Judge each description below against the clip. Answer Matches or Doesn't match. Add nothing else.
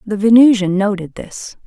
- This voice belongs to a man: Doesn't match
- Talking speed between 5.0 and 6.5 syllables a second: Doesn't match